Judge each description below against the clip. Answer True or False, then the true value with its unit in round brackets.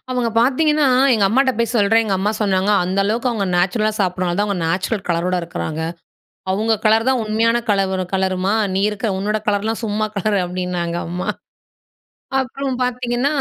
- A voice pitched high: True (210 Hz)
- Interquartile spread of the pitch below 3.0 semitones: False (3.6 semitones)